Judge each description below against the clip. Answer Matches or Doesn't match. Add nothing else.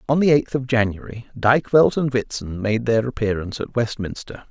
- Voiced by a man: Matches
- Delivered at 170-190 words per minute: Matches